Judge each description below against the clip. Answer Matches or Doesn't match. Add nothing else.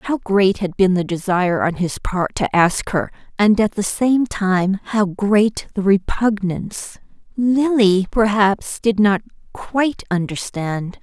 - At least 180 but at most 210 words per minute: Doesn't match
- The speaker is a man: Doesn't match